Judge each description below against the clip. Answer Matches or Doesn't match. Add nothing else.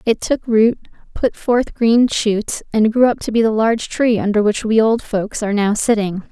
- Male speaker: Doesn't match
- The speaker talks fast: Matches